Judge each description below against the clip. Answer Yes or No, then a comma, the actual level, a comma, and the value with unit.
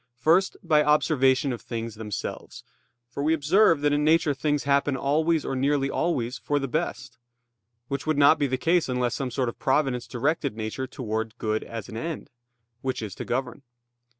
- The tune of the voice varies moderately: Yes, average, 3.5 semitones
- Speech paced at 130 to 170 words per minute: No, average, 180 wpm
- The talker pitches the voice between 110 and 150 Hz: Yes, medium, 140 Hz